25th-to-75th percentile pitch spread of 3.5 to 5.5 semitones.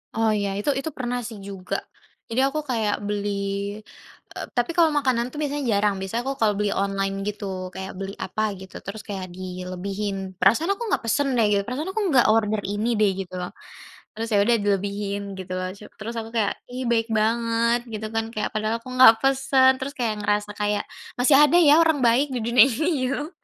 Yes: average, 3.8 semitones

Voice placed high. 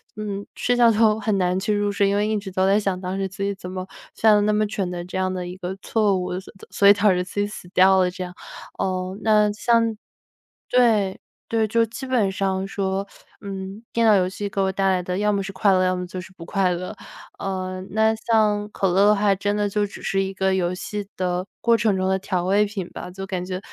Yes: high, 195 Hz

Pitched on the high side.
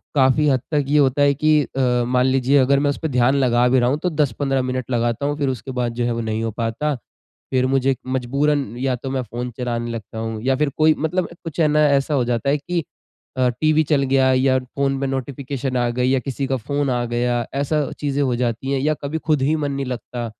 No: low, 135 Hz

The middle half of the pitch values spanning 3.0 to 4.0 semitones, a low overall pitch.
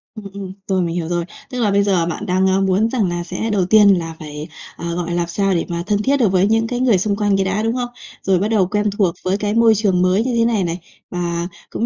No: average, 3.5 semitones; high, 195 Hz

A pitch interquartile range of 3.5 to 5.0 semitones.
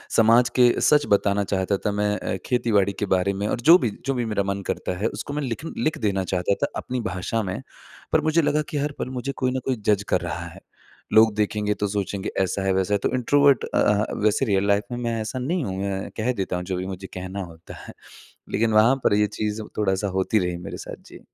Yes: average, 4.0 semitones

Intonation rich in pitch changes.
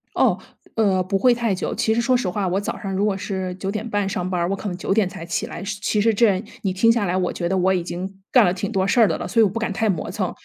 No: average, 2.7 semitones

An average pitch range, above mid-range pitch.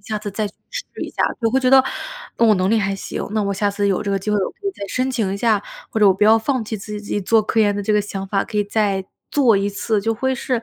No: narrow, 2.2 semitones; high, 210 Hz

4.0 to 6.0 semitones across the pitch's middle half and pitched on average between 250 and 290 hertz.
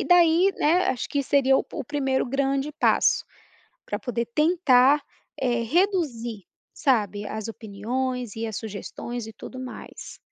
Yes: average, 4.3 semitones; very high, 255 Hz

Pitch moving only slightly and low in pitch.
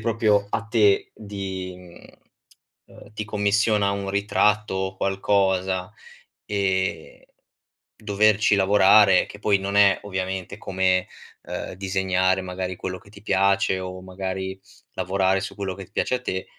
Yes: narrow, 1.5 semitones; very low, 95 Hz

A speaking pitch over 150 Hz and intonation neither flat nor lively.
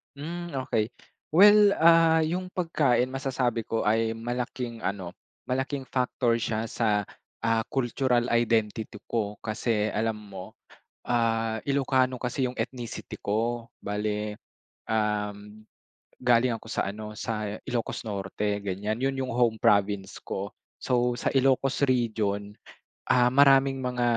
No: low, 115 Hz; average, 3.4 semitones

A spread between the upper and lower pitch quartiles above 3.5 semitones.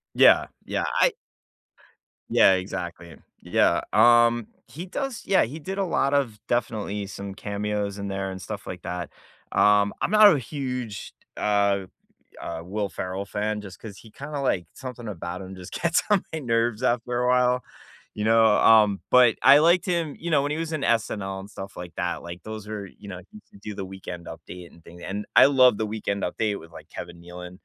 Yes: average, 4.7 semitones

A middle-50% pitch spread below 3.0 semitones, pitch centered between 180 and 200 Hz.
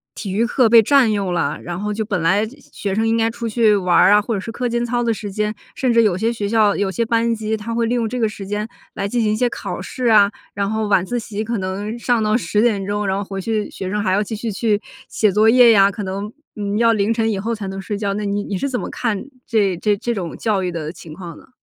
No: narrow, 2.5 semitones; high, 210 Hz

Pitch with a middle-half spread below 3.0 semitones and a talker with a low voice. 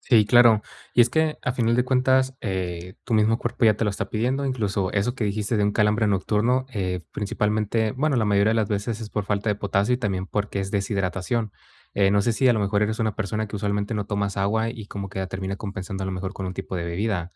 Yes: narrow, 2.6 semitones; low, 105 Hz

